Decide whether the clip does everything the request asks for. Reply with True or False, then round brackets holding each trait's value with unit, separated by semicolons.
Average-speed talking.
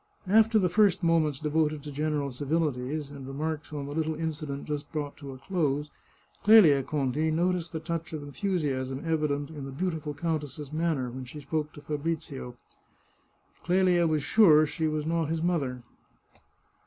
True (165 wpm)